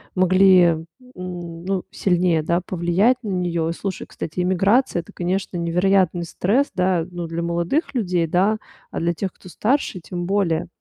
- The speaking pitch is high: No, medium, 180 Hz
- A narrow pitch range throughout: Yes, narrow, 2.1 semitones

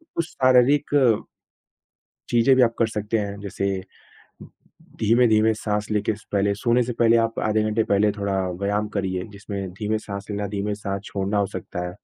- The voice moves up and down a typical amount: No, narrow, 2.2 semitones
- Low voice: Yes, low, 105 Hz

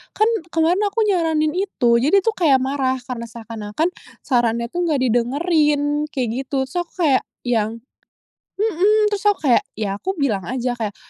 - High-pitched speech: Yes, very high, 280 Hz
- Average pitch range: No, wide, 6.6 semitones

